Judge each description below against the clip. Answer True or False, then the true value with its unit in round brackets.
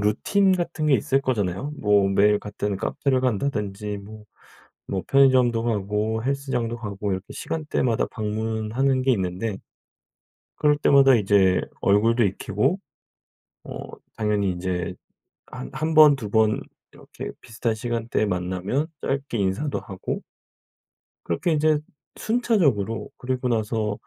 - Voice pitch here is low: True (110 Hz)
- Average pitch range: True (4.9 semitones)